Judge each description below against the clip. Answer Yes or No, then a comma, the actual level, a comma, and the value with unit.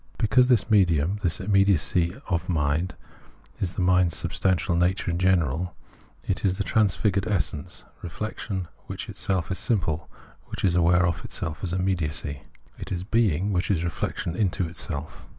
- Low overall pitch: Yes, very low, 90 Hz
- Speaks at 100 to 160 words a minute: Yes, average, 155 wpm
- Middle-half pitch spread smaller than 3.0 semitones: Yes, narrow, 2.6 semitones